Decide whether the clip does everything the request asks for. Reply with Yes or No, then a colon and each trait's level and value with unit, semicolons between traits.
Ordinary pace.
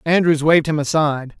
Yes: average, 170 wpm